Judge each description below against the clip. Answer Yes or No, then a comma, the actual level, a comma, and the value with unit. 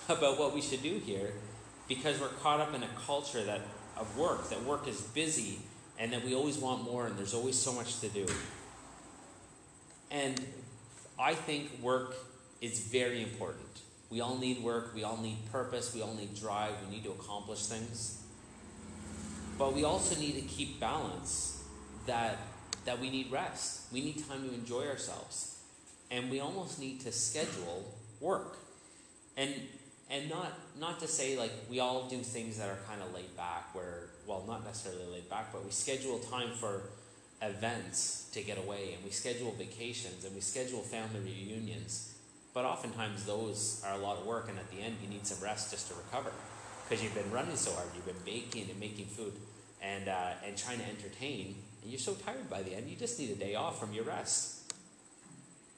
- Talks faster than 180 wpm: Yes, average, 190 wpm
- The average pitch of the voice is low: Yes, low, 115 Hz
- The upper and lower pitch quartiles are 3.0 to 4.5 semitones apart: Yes, average, 4.0 semitones